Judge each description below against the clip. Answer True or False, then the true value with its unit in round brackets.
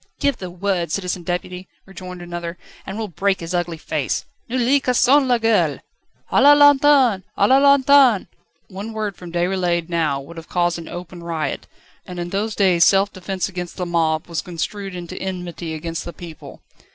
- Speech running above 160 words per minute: True (180 wpm)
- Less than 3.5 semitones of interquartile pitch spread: False (3.8 semitones)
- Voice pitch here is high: False (180 Hz)